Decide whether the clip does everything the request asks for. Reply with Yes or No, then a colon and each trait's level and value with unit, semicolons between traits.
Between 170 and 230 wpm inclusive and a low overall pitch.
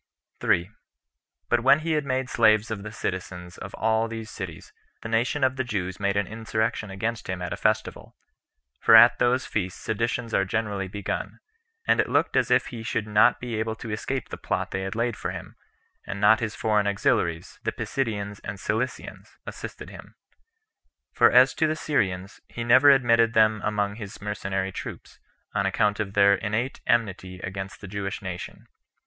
Yes: average, 180 wpm; low, 110 Hz